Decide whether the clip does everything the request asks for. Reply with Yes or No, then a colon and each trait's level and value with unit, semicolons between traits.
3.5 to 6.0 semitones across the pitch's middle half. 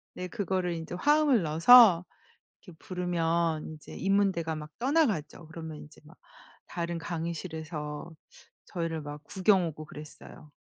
No: average, 2.9 semitones